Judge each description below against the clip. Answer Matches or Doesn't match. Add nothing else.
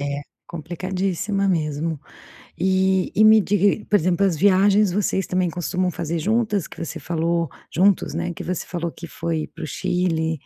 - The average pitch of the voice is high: Doesn't match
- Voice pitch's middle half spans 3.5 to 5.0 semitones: Doesn't match